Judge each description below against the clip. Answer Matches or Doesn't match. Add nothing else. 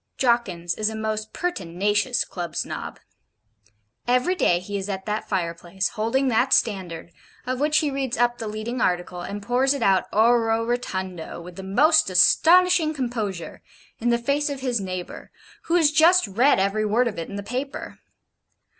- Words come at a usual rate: Matches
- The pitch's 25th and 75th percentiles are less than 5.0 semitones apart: Doesn't match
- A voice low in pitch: Doesn't match